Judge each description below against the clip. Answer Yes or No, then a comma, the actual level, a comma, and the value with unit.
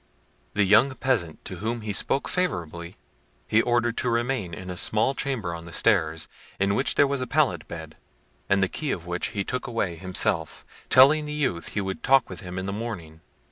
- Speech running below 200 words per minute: No, fast, 205 wpm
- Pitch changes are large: Yes, wide, 6.5 semitones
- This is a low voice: Yes, low, 100 Hz